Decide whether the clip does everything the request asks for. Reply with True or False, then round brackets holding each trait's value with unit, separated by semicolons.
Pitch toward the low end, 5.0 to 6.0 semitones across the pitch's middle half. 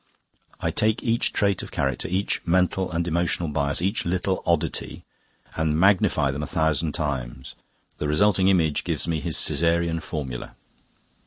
False (85 Hz; 3.7 semitones)